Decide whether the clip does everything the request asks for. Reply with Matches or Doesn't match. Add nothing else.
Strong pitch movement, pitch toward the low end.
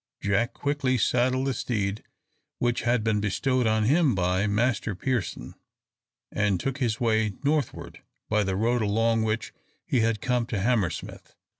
Doesn't match